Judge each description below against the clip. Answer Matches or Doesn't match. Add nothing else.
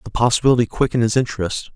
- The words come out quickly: Doesn't match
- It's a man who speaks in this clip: Matches